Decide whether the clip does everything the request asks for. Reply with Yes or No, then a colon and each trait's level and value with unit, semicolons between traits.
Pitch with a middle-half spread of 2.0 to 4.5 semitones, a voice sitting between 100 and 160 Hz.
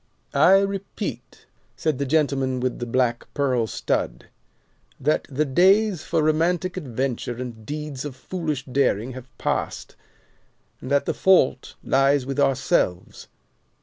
Yes: average, 3.8 semitones; medium, 140 Hz